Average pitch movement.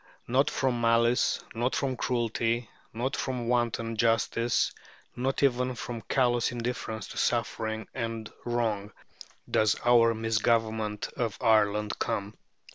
No: narrow, 1.7 semitones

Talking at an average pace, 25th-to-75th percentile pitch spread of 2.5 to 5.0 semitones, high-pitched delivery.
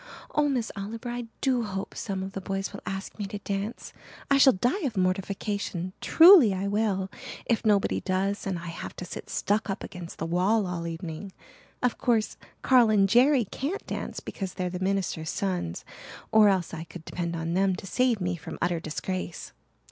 Yes: average, 195 wpm; average, 3.5 semitones; high, 195 Hz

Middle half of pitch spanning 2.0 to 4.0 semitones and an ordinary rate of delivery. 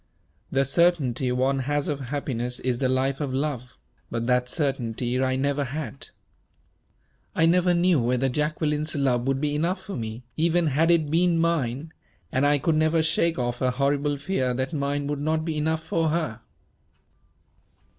Yes: average, 3.6 semitones; average, 165 wpm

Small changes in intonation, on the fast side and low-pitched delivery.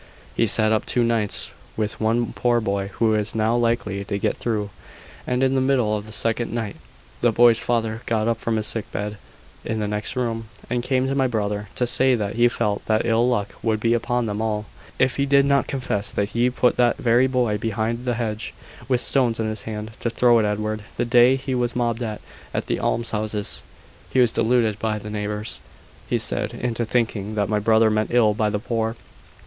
Yes: narrow, 2.2 semitones; fast, 210 wpm; low, 115 Hz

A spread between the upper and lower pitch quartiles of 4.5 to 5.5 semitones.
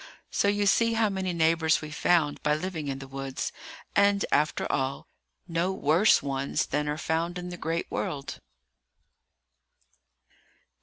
No: average, 4.1 semitones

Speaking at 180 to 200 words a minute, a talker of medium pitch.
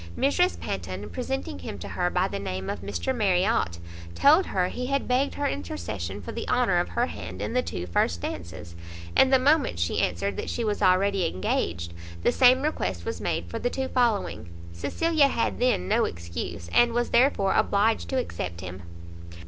Yes: average, 190 wpm; medium, 180 Hz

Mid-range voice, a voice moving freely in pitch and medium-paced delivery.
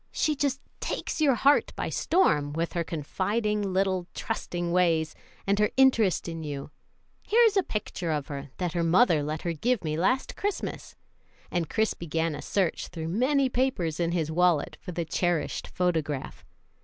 Yes: medium, 175 Hz; wide, 5.7 semitones; average, 170 wpm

